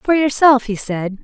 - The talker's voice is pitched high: Yes, high, 245 Hz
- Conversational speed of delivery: Yes, average, 195 wpm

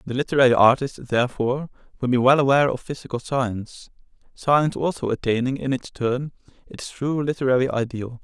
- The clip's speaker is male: Yes, male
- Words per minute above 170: No, average, 155 wpm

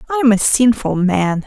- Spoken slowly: No, fast, 205 wpm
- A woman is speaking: Yes, female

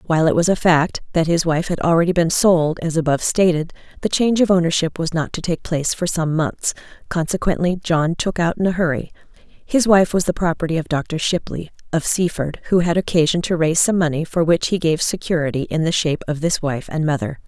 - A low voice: No, medium, 165 Hz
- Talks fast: Yes, fast, 220 wpm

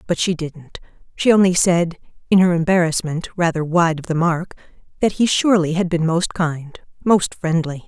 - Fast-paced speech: No, average, 160 wpm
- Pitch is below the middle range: No, medium, 170 Hz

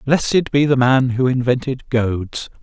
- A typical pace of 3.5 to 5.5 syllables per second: Yes, 4.2 syllables/s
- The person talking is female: No, male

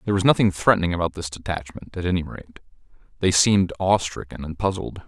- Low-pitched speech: Yes, very low, 90 Hz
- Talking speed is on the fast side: No, average, 175 wpm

